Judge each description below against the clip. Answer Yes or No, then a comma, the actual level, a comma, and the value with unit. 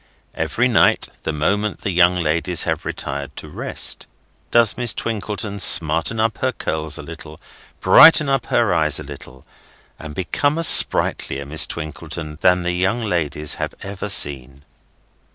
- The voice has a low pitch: Yes, very low, 90 Hz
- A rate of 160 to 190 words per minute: No, average, 150 wpm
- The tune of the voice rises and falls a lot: Yes, wide, 5.8 semitones